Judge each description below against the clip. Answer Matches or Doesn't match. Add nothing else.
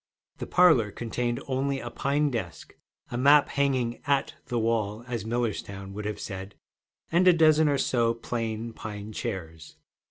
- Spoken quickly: Doesn't match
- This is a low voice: Matches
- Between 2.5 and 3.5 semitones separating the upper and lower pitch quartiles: Doesn't match